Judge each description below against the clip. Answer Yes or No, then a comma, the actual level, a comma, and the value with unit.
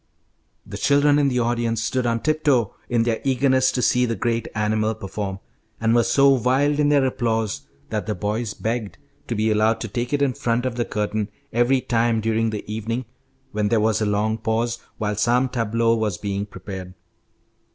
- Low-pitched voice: Yes, low, 115 Hz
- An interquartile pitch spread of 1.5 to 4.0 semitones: Yes, narrow, 2.5 semitones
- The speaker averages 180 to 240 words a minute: Yes, average, 190 wpm